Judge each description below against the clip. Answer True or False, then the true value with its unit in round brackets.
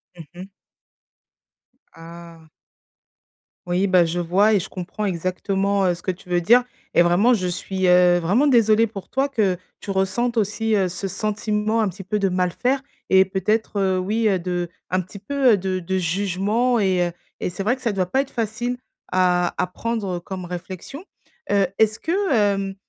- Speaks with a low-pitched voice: False (195 Hz)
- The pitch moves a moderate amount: True (3.3 semitones)